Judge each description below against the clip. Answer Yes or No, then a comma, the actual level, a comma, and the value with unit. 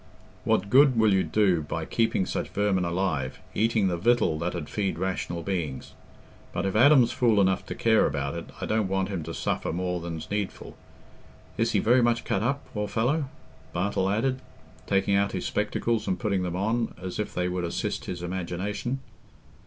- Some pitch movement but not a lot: Yes, average, 4.0 semitones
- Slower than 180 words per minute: No, average, 185 wpm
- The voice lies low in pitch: Yes, very low, 95 Hz